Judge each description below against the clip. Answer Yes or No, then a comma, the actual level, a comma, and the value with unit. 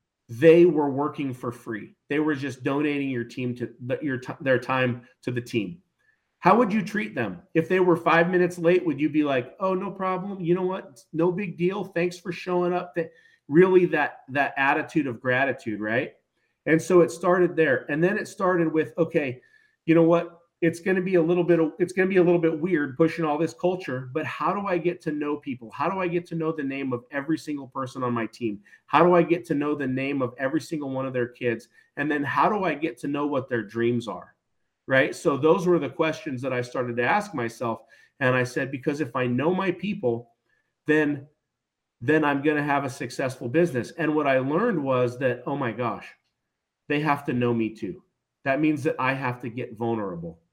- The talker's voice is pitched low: No, medium, 150 Hz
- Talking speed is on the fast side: Yes, fast, 225 wpm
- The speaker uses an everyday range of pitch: Yes, average, 4.9 semitones